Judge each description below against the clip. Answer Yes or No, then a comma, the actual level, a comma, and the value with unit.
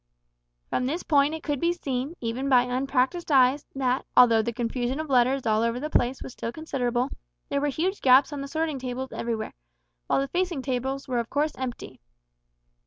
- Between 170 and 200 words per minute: Yes, average, 190 wpm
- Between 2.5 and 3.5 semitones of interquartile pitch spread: Yes, average, 2.8 semitones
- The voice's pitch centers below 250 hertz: No, very high, 265 Hz